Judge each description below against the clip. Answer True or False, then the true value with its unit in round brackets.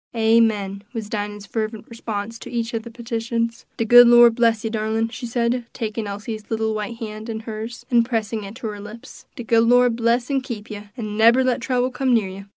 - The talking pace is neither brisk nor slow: False (215 wpm)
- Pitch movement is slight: True (1.7 semitones)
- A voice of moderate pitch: False (225 Hz)